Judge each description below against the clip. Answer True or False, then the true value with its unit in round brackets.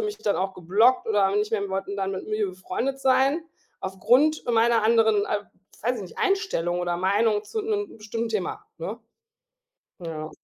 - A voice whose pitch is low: False (215 Hz)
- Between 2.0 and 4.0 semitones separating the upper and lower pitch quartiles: False (4.7 semitones)